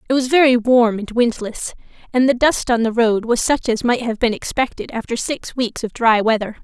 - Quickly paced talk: Yes, fast, 225 wpm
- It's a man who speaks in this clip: No, female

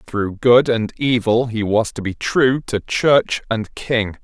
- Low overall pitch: Yes, low, 115 Hz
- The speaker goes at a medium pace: Yes, average, 185 wpm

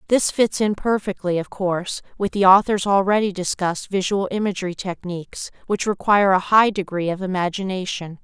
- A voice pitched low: No, high, 190 Hz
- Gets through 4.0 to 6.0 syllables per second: Yes, 5.5 syllables/s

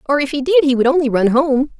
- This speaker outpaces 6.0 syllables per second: Yes, 6.4 syllables/s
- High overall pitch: Yes, very high, 270 Hz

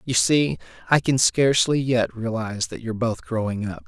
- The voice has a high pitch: No, low, 115 Hz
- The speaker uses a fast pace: No, average, 155 wpm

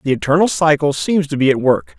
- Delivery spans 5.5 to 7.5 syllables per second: Yes, 5.9 syllables/s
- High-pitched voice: No, medium, 145 Hz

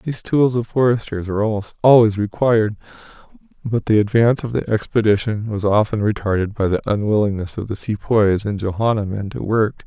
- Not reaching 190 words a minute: Yes, average, 170 wpm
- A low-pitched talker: Yes, low, 110 Hz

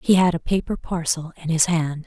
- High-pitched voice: No, medium, 165 Hz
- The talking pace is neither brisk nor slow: No, fast, 235 wpm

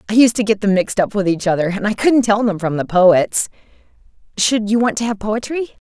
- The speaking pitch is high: Yes, high, 210 Hz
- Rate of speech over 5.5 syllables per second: Yes, 5.8 syllables/s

